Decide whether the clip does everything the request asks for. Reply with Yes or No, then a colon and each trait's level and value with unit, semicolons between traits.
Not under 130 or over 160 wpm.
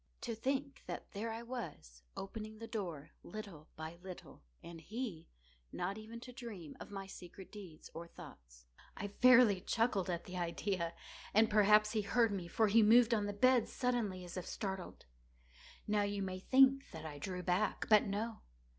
No: average, 170 wpm